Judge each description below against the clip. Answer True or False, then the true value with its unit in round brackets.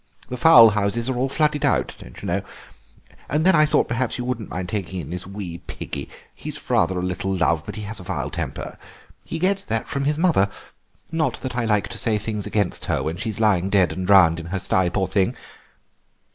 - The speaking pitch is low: True (105 Hz)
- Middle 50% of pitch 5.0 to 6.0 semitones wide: True (5.3 semitones)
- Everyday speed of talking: False (215 wpm)